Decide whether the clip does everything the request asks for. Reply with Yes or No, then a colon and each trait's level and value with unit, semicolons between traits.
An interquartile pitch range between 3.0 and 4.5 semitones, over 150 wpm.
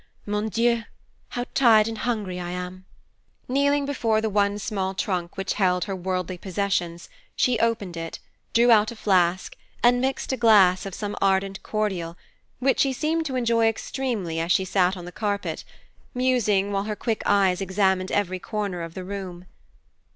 Yes: average, 3.8 semitones; average, 170 wpm